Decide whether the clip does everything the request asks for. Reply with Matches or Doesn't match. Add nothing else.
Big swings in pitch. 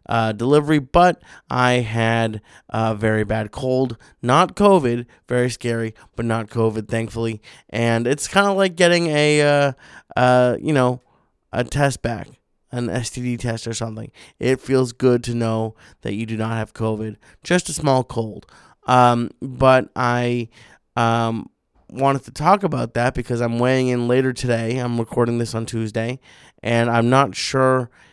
Doesn't match